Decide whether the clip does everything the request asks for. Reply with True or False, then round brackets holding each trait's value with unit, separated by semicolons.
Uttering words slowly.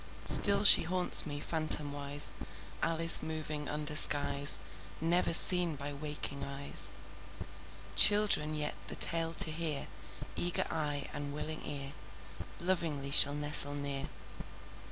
True (115 wpm)